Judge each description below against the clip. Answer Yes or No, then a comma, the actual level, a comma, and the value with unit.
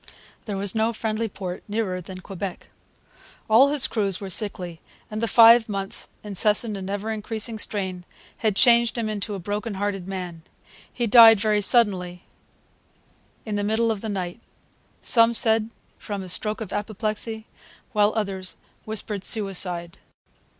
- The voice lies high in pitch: Yes, high, 210 Hz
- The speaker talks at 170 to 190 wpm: No, average, 150 wpm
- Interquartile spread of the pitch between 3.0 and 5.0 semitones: No, narrow, 2.5 semitones